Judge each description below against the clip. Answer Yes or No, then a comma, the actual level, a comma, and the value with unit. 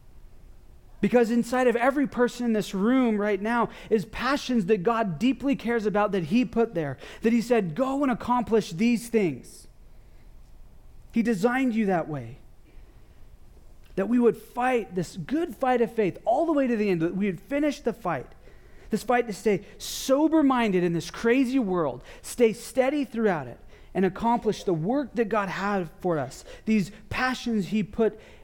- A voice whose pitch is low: No, high, 225 Hz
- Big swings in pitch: No, average, 4.3 semitones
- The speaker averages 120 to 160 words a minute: No, average, 170 wpm